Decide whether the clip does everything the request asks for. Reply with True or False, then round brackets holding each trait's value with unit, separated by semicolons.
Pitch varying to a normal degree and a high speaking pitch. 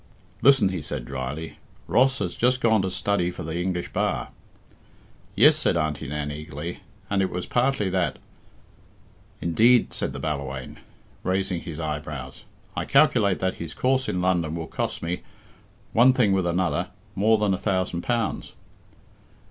False (4.8 semitones; 90 Hz)